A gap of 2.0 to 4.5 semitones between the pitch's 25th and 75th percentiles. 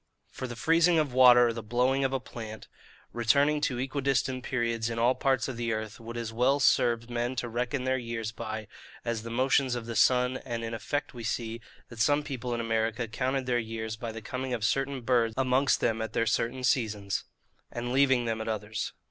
Yes: narrow, 2.4 semitones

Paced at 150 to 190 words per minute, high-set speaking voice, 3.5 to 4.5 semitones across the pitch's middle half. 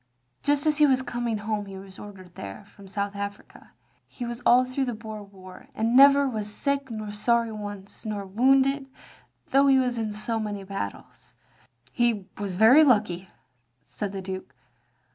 Yes: average, 175 wpm; high, 215 Hz; average, 4.1 semitones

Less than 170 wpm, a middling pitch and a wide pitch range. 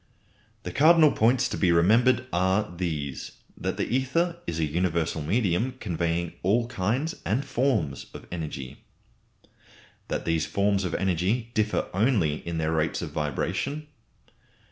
No: average, 140 wpm; very low, 95 Hz; wide, 7.0 semitones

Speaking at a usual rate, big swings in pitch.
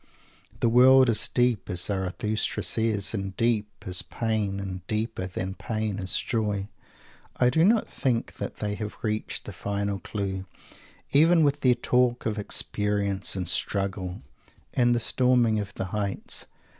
No: average, 150 wpm; average, 3.5 semitones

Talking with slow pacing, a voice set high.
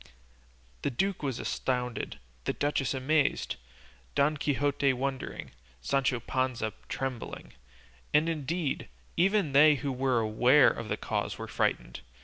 No: slow, 125 wpm; low, 135 Hz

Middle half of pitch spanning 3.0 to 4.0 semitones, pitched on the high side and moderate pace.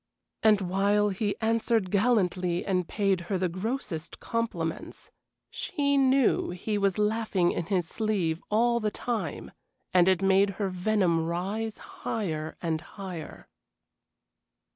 No: average, 3.6 semitones; high, 195 Hz; slow, 125 wpm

